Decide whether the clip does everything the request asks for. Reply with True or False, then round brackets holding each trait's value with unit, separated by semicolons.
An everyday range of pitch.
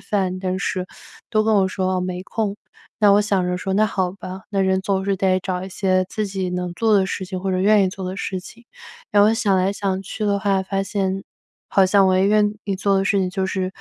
False (1.4 semitones)